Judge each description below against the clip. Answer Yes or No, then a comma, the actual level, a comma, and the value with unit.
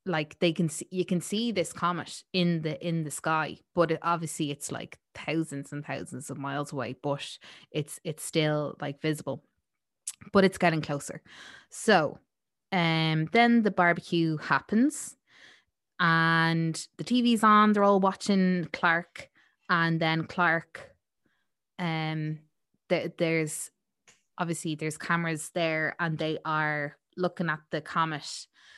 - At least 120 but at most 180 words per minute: Yes, average, 140 wpm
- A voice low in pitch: No, medium, 165 Hz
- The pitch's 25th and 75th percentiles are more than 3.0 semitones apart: No, narrow, 2.5 semitones